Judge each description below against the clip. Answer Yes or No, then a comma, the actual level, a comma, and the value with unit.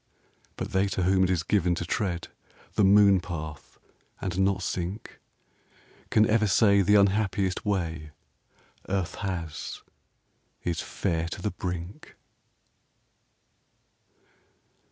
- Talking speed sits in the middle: No, slow, 115 wpm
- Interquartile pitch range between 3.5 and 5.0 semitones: No, narrow, 2.6 semitones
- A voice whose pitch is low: Yes, very low, 95 Hz